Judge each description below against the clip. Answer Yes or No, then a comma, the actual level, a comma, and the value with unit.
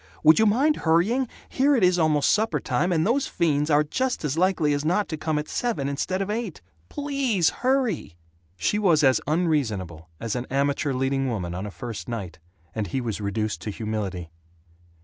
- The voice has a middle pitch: Yes, medium, 150 Hz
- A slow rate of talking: No, average, 185 wpm